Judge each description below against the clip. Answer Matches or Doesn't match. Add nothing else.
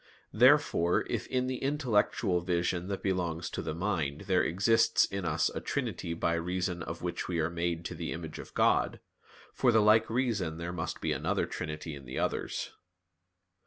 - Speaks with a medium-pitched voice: Doesn't match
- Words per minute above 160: Matches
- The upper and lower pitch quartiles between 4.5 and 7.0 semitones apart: Doesn't match